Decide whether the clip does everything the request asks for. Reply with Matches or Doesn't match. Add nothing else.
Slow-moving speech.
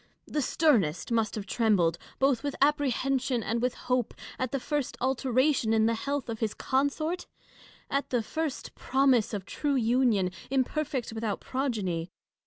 Doesn't match